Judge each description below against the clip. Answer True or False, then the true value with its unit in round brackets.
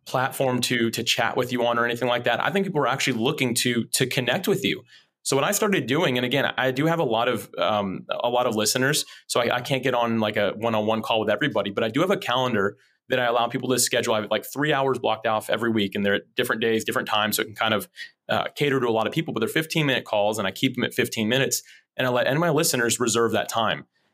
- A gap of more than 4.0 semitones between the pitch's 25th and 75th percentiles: False (2.8 semitones)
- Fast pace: True (285 wpm)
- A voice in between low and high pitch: False (125 Hz)